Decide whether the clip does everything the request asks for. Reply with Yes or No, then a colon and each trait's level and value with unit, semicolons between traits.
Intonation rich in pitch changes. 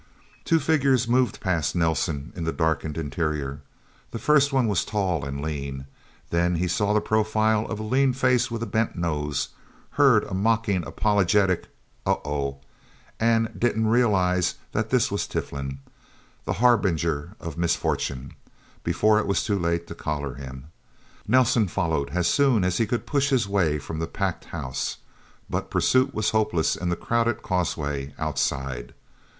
Yes: wide, 6.6 semitones